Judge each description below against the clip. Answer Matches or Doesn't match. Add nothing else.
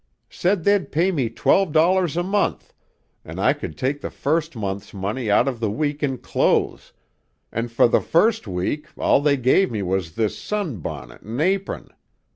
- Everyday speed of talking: Matches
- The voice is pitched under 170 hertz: Matches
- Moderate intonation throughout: Doesn't match